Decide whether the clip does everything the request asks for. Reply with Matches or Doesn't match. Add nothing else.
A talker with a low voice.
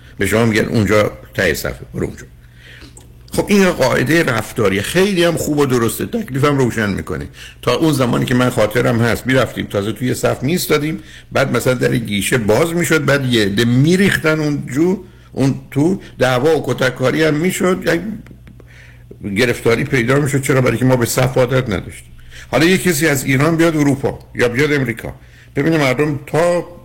Matches